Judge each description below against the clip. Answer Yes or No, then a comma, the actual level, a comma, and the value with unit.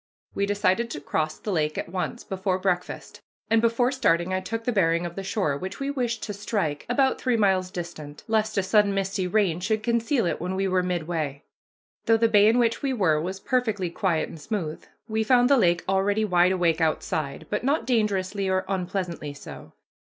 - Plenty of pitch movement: No, average, 4.1 semitones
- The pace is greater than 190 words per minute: Yes, average, 200 wpm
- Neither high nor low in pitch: No, high, 195 Hz